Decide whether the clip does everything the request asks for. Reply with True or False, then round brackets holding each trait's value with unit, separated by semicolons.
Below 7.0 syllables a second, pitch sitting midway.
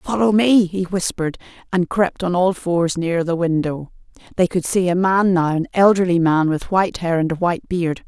True (5.2 syllables/s; 180 Hz)